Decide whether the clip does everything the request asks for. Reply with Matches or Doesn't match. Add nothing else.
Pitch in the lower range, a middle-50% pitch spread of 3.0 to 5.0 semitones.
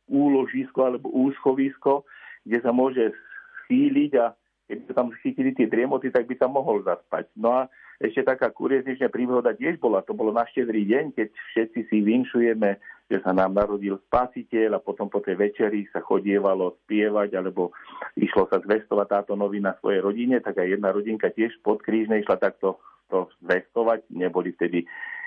Matches